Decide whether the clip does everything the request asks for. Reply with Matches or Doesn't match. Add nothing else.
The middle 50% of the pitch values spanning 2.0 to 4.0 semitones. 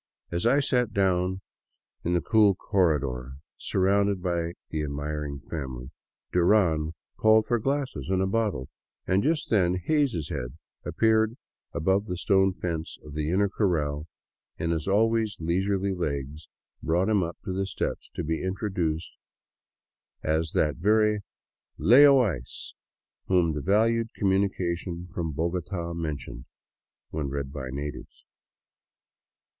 Doesn't match